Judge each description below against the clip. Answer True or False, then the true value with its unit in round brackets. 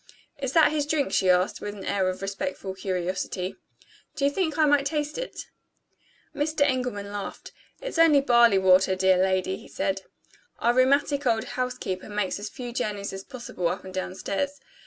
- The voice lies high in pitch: True (215 Hz)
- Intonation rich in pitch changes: True (6.9 semitones)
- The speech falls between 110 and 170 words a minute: False (180 wpm)